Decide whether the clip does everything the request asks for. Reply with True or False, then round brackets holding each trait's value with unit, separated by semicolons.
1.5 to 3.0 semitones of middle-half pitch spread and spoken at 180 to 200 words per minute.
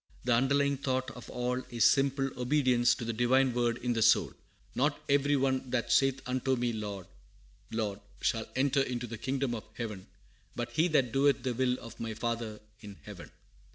True (2.6 semitones; 185 wpm)